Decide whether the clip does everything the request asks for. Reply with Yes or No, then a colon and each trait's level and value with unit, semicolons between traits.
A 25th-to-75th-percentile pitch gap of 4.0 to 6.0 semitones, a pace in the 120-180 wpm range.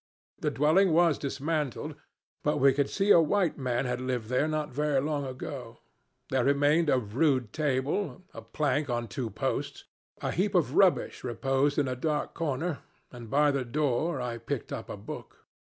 No: average, 3.3 semitones; average, 175 wpm